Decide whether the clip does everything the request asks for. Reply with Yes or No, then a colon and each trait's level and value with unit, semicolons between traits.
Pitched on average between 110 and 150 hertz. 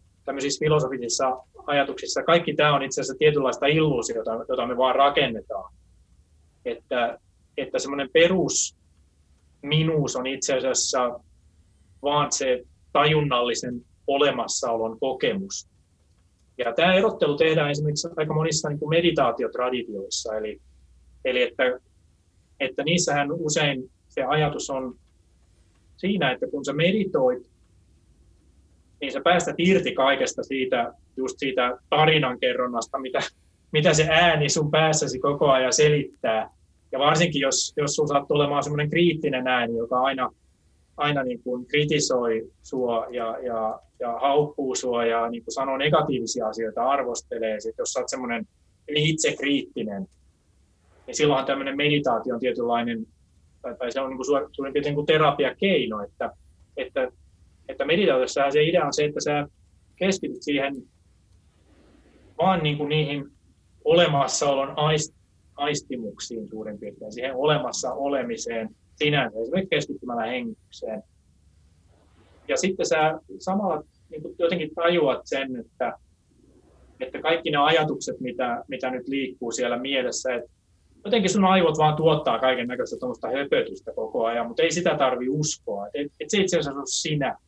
Yes: low, 135 Hz